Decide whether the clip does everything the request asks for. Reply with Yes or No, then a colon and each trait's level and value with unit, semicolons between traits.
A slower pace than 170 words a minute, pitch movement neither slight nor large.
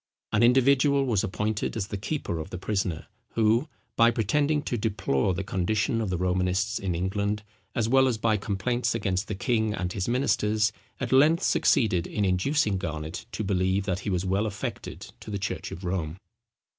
No: average, 180 wpm; average, 4.0 semitones